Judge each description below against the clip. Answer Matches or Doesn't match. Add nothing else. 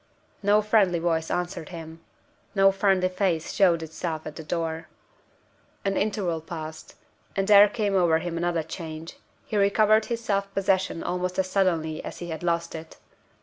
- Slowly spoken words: Doesn't match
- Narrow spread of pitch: Doesn't match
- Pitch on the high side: Doesn't match